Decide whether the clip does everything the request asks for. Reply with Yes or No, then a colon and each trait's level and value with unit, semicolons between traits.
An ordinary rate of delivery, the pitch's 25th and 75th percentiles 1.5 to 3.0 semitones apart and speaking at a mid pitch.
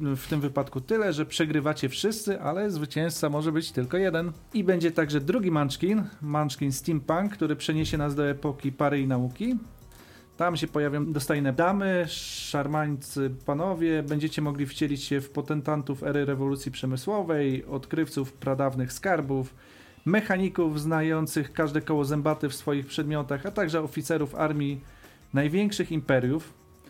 Yes: average, 135 wpm; average, 2.7 semitones; medium, 150 Hz